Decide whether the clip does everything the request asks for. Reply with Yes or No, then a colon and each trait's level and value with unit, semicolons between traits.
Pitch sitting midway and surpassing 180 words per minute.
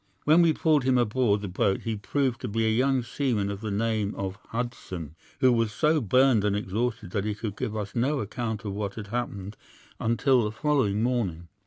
No: low, 110 Hz; fast, 205 wpm